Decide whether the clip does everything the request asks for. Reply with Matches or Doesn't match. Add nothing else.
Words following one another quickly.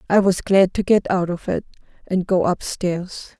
Doesn't match